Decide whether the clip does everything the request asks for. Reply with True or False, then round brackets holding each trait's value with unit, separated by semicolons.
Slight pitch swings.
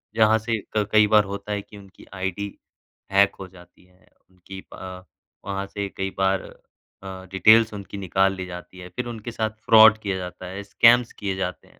True (2.3 semitones)